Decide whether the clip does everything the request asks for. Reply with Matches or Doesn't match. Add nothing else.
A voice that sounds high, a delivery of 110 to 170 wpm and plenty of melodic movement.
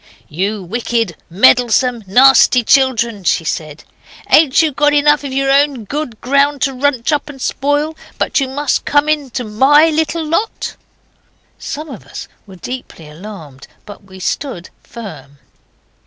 Matches